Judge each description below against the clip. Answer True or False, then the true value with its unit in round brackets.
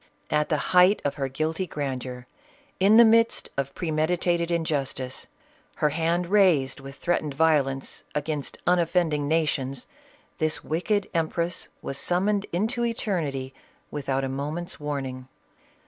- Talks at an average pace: False (130 wpm)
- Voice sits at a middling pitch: True (155 Hz)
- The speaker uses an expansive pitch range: False (4.2 semitones)